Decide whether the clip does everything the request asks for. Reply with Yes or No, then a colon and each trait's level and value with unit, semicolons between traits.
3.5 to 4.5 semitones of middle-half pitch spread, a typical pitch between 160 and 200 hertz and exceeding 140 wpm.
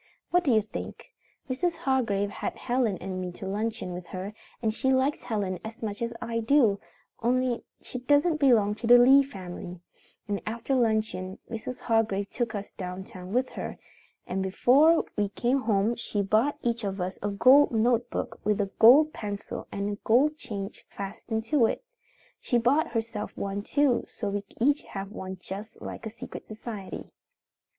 No: average, 4.0 semitones; high, 225 Hz; average, 175 wpm